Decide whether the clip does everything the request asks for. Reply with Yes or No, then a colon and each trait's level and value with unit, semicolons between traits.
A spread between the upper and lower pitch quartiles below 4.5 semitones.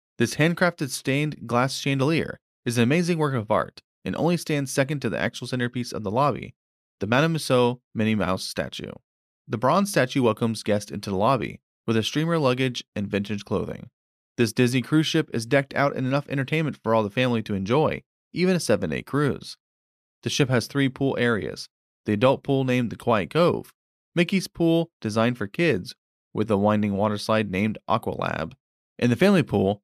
No: average, 5.1 semitones